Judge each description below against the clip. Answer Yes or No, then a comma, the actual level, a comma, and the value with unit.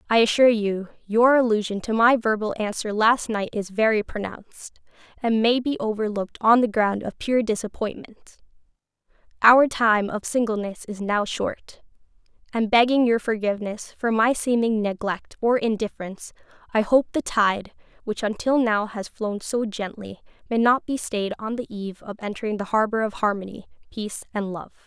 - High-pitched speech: Yes, high, 220 Hz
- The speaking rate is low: No, average, 165 wpm